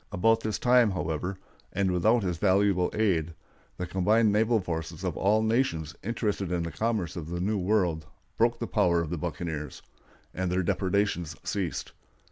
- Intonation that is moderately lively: Yes, average, 4.0 semitones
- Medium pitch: No, very low, 95 Hz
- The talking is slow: No, average, 170 wpm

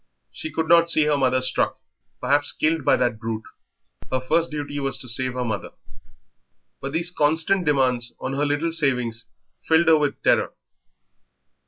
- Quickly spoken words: No, average, 165 wpm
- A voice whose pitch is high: No, medium, 145 Hz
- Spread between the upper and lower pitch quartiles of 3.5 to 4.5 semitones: Yes, average, 3.9 semitones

